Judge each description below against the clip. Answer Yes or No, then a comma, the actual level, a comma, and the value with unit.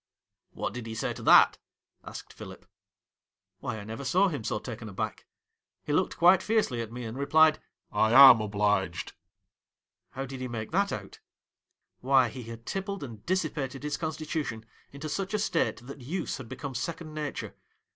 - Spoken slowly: No, average, 200 wpm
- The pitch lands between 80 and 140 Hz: Yes, low, 135 Hz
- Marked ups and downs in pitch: Yes, wide, 5.8 semitones